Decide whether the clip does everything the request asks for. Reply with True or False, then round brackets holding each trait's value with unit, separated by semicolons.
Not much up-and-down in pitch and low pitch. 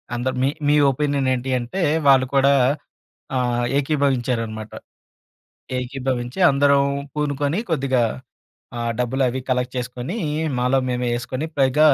True (2.3 semitones; 130 Hz)